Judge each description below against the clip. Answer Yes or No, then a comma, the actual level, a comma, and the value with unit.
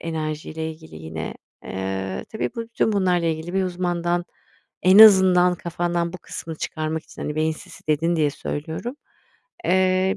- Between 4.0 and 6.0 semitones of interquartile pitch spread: No, average, 2.9 semitones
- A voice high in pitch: No, medium, 170 Hz